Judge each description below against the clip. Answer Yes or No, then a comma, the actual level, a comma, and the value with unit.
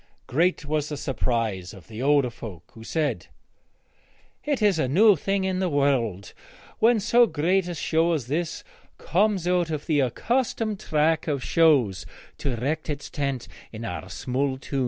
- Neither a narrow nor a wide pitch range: No, wide, 6.1 semitones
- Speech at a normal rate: Yes, average, 165 wpm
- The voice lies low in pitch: No, medium, 150 Hz